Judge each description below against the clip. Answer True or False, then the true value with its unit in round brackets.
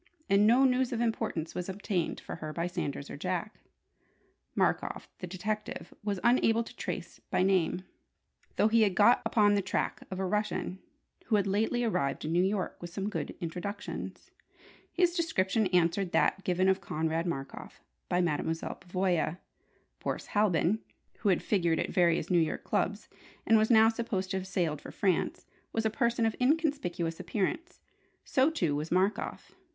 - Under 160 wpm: False (165 wpm)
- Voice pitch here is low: False (190 Hz)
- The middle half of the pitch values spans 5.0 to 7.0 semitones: False (4.1 semitones)